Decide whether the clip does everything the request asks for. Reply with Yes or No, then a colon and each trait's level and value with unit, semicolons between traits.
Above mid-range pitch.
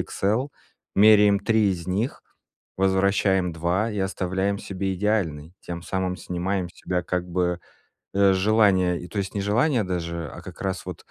No: very low, 95 Hz